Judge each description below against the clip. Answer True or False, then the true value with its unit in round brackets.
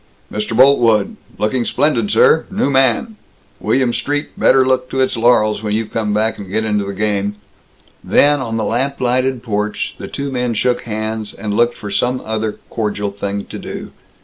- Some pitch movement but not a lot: True (3.5 semitones)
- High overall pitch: False (115 Hz)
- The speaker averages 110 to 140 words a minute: False (180 wpm)